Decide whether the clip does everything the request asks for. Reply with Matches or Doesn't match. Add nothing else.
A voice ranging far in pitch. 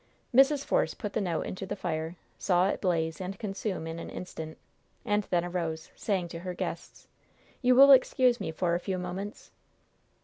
Doesn't match